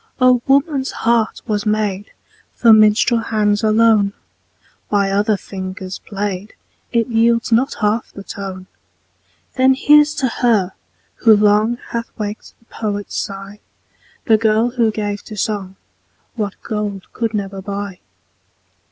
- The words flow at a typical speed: No, slow, 130 wpm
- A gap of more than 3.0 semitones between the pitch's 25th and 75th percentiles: No, narrow, 2.4 semitones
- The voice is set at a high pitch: Yes, high, 215 Hz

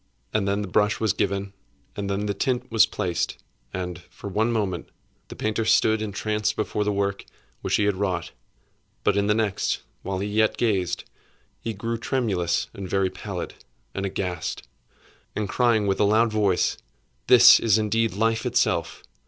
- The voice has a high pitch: No, low, 105 Hz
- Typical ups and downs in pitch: No, narrow, 2.0 semitones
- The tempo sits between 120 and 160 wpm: No, average, 170 wpm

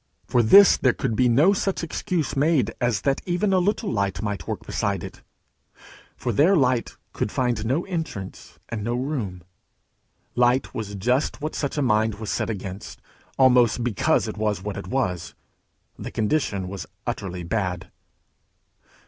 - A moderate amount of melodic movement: No, wide, 5.7 semitones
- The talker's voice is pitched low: Yes, low, 120 Hz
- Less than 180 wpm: Yes, average, 160 wpm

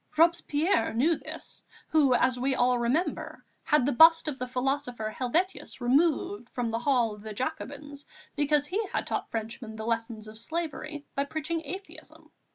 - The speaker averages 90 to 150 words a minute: No, average, 165 wpm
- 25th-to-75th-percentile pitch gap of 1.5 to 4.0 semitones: No, average, 4.6 semitones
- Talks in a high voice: Yes, very high, 270 Hz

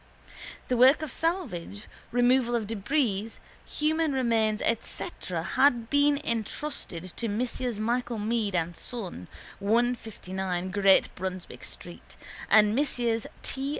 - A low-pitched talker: No, high, 230 Hz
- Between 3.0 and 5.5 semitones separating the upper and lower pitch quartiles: Yes, average, 4.2 semitones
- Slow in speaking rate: Yes, slow, 115 wpm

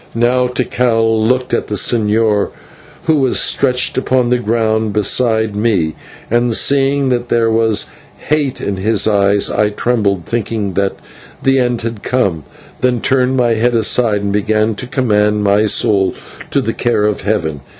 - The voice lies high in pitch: No, low, 115 Hz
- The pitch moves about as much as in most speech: Yes, average, 3.0 semitones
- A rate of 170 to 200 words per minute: No, average, 160 wpm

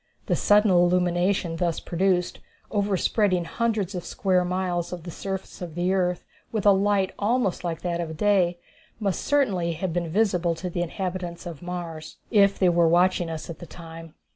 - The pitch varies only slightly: Yes, narrow, 2.1 semitones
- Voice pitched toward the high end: No, medium, 180 Hz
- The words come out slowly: No, average, 175 wpm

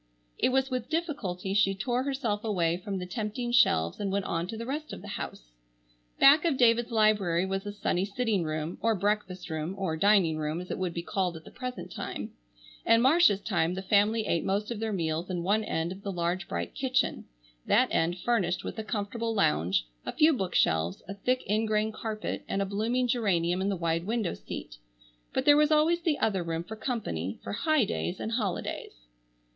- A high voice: Yes, high, 200 Hz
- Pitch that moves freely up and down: No, average, 4.8 semitones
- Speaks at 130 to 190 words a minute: No, average, 200 wpm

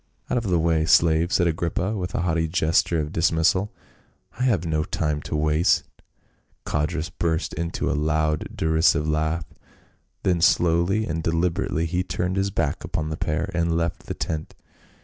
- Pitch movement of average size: No, narrow, 2.0 semitones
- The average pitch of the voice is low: Yes, very low, 80 Hz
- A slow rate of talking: No, average, 170 wpm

